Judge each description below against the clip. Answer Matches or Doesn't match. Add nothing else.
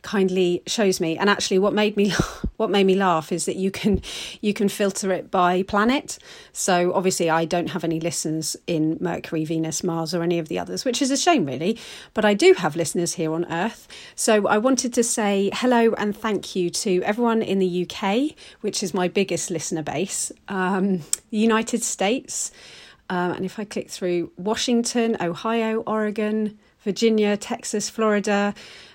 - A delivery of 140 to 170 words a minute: Doesn't match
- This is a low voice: Doesn't match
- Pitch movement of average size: Matches